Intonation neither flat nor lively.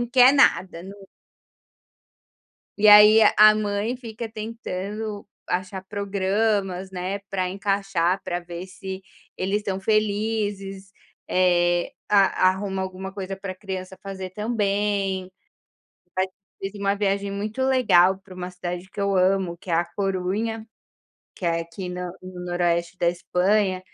No: narrow, 2.0 semitones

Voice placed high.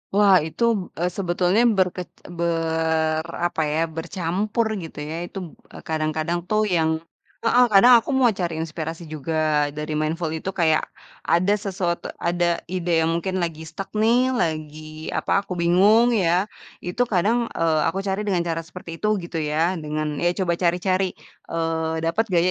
No: medium, 170 Hz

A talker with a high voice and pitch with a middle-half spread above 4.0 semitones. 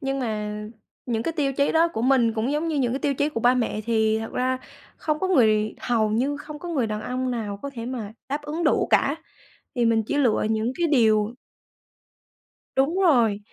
Yes: very high, 250 Hz; average, 4.6 semitones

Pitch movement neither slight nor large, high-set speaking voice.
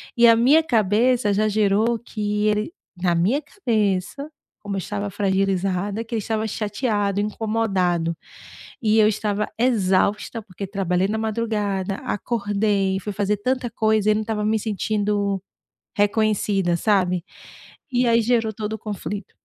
No: narrow, 2.0 semitones; high, 210 Hz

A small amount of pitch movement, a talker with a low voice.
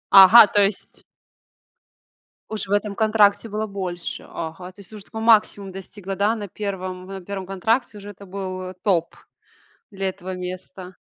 No: narrow, 2.0 semitones; high, 195 Hz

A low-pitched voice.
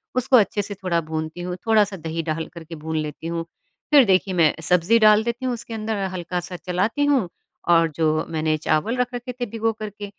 No: medium, 185 Hz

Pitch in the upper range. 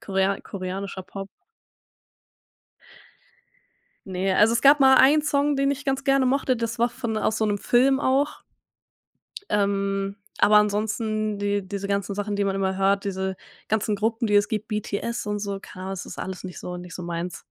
Yes: high, 205 Hz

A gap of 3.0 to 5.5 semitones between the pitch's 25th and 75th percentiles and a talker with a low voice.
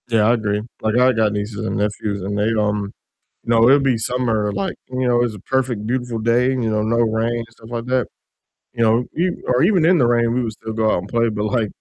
No: narrow, 2.5 semitones; low, 115 Hz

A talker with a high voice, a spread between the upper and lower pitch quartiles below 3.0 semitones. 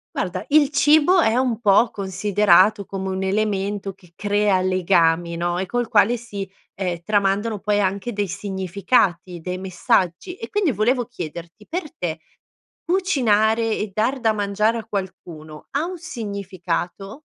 No: high, 205 Hz; average, 3.7 semitones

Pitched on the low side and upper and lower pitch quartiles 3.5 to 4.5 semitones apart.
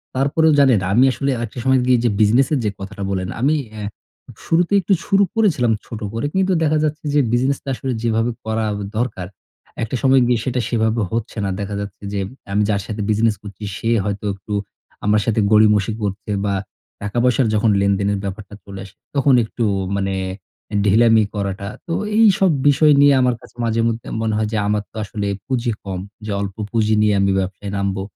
Yes: low, 110 Hz; average, 4.2 semitones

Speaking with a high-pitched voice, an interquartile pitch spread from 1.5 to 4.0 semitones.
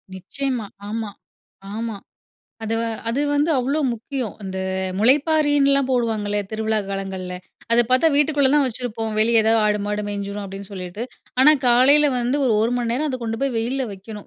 No: high, 230 Hz; average, 4.6 semitones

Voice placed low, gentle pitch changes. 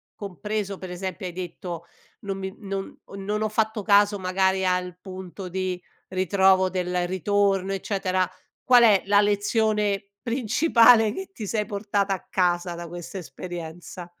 No: high, 195 Hz; narrow, 2.1 semitones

